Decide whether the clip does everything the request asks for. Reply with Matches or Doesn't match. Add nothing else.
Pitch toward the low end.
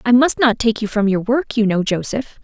Doesn't match